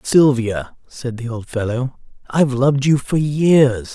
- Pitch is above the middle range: No, low, 130 Hz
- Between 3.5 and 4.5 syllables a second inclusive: Yes, 4.1 syllables/s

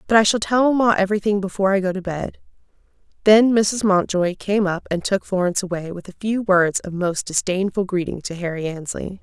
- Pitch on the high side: Yes, high, 195 Hz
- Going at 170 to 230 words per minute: Yes, average, 200 wpm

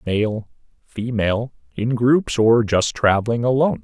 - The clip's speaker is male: Yes, male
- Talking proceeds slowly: Yes, slow, 125 wpm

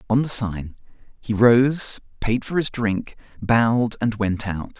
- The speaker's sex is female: No, male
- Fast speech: No, average, 165 wpm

